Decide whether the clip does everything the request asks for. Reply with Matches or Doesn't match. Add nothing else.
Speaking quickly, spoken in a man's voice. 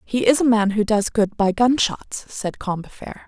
Doesn't match